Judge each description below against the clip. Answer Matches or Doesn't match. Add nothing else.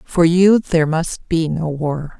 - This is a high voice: Doesn't match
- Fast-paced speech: Doesn't match